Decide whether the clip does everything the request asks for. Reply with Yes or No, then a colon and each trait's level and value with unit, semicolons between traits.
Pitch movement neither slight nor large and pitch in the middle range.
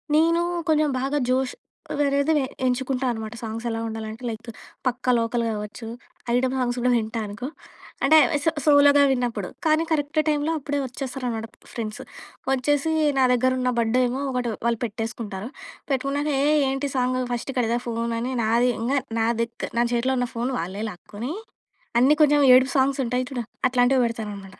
No: average, 3.0 semitones; very high, 250 Hz